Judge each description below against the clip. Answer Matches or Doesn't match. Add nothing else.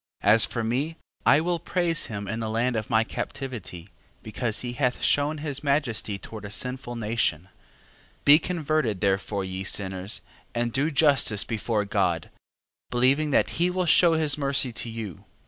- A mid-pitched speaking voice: Doesn't match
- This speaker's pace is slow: Doesn't match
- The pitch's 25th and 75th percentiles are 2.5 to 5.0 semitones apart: Doesn't match